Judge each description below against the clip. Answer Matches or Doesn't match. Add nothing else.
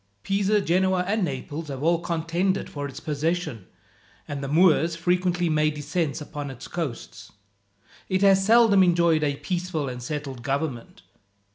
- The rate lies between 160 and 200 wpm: Doesn't match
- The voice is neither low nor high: Matches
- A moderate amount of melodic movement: Matches